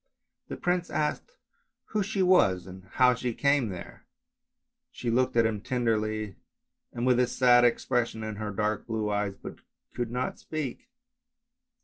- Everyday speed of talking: Yes, average, 155 wpm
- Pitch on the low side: Yes, low, 120 Hz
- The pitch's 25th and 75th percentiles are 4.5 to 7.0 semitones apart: No, average, 3.2 semitones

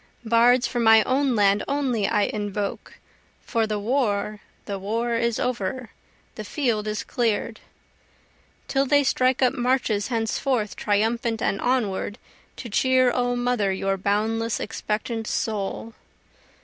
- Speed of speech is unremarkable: No, slow, 130 wpm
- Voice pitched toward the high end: Yes, high, 225 Hz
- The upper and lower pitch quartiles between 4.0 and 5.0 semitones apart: No, average, 3.0 semitones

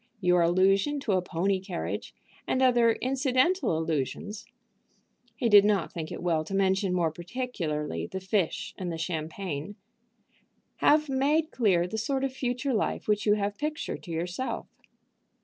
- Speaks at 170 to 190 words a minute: No, average, 150 wpm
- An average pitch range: No, wide, 6.4 semitones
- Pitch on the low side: No, high, 195 Hz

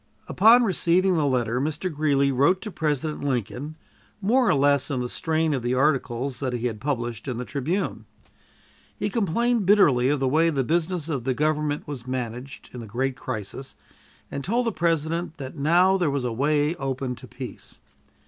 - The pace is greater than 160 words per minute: Yes, average, 185 wpm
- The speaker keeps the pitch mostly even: No, average, 4.6 semitones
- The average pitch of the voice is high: No, medium, 145 Hz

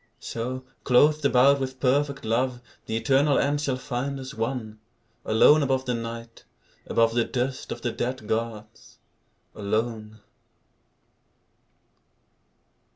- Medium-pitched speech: No, low, 125 Hz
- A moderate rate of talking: No, slow, 115 wpm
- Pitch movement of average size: Yes, average, 3.0 semitones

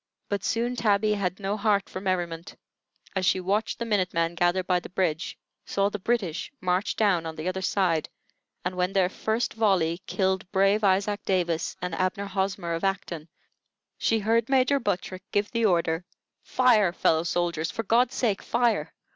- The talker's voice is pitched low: No, high, 190 Hz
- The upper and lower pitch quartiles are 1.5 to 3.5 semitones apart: Yes, average, 3.0 semitones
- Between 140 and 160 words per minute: No, average, 170 wpm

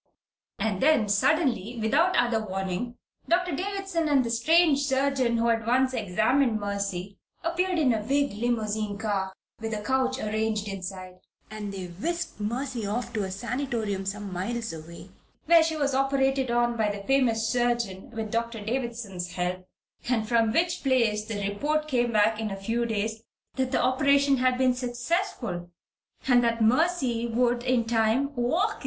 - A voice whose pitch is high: Yes, high, 235 Hz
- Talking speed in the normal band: Yes, average, 165 wpm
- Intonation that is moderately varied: Yes, average, 4.2 semitones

